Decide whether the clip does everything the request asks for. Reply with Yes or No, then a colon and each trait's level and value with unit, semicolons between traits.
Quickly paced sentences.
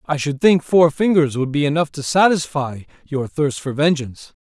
No: average, 190 wpm